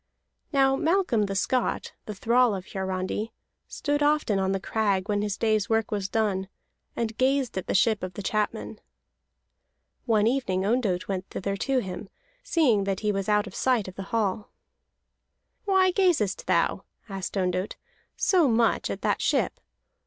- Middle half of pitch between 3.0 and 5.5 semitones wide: Yes, average, 4.6 semitones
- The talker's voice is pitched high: Yes, high, 210 Hz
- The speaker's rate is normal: Yes, average, 160 wpm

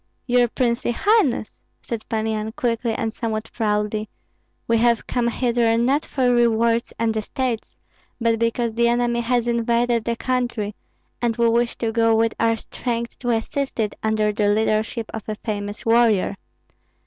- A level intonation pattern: Yes, narrow, 1.5 semitones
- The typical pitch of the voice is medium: No, high, 230 Hz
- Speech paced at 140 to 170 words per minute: Yes, average, 160 wpm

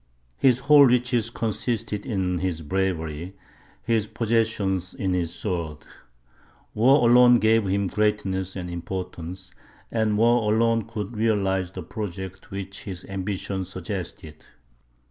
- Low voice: Yes, low, 100 Hz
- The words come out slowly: Yes, slow, 120 wpm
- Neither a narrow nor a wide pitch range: Yes, average, 3.6 semitones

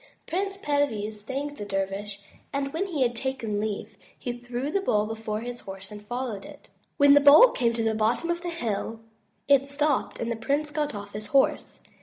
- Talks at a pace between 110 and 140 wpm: No, average, 200 wpm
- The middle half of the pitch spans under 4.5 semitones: No, average, 5.2 semitones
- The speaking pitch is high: Yes, high, 245 Hz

